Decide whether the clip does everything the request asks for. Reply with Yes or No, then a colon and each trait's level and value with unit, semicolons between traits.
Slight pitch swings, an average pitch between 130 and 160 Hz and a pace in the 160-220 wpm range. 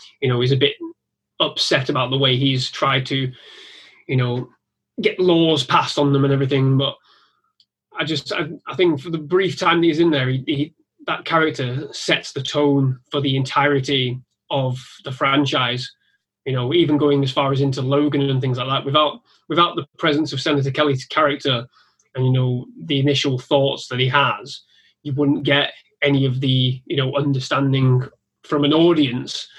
Yes: narrow, 2.2 semitones; medium, 140 Hz; average, 185 wpm